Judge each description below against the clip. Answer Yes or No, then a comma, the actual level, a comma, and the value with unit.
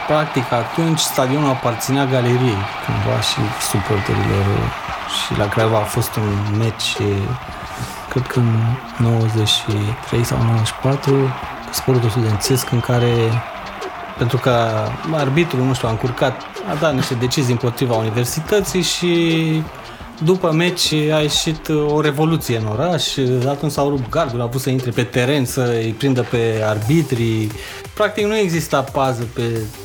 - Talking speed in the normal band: Yes, average, 135 wpm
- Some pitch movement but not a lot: Yes, average, 4.4 semitones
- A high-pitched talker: No, low, 125 Hz